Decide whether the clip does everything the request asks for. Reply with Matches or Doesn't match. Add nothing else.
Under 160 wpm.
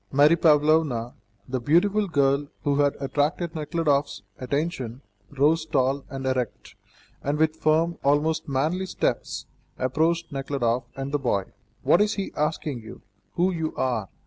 Matches